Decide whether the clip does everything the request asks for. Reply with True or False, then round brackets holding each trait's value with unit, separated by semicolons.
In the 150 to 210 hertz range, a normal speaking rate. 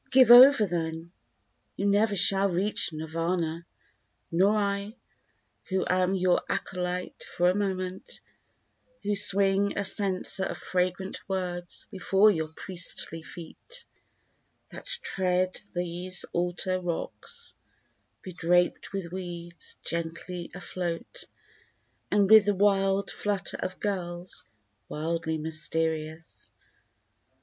False (185 Hz; 105 wpm)